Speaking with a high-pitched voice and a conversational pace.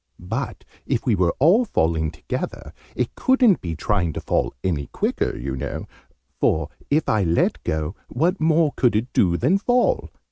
No: low, 110 Hz; average, 170 wpm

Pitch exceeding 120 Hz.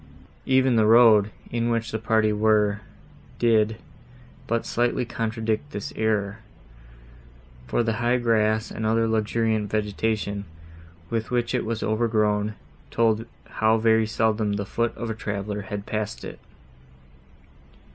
No: low, 110 Hz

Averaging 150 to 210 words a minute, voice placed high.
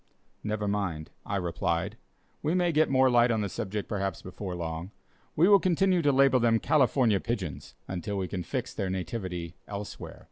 No: average, 175 wpm; low, 105 Hz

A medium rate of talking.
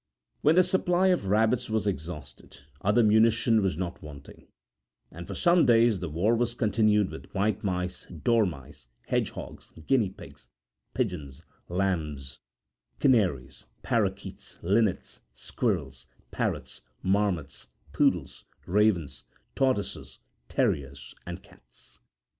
No: slow, 110 wpm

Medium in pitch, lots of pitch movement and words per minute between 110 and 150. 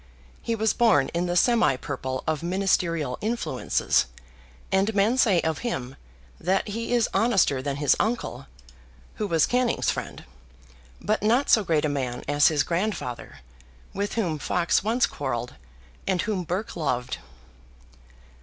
Yes: medium, 180 Hz; wide, 7.1 semitones; average, 145 wpm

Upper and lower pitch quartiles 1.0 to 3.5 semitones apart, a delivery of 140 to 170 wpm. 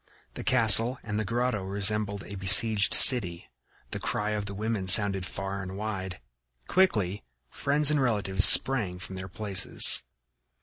Yes: average, 2.9 semitones; average, 145 wpm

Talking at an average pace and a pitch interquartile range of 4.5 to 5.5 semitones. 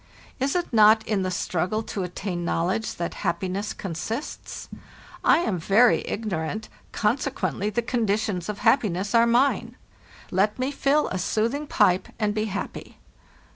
No: average, 145 wpm; average, 3.9 semitones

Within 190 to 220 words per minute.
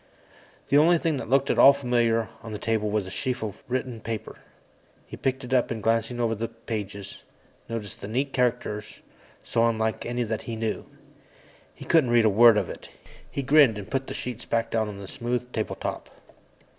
Yes: average, 200 wpm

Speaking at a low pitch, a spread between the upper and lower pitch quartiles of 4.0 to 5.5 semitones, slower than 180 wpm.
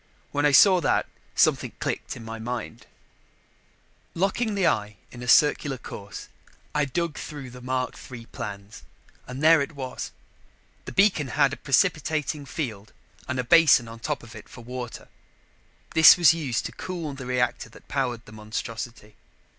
Yes: low, 130 Hz; average, 4.6 semitones; average, 160 wpm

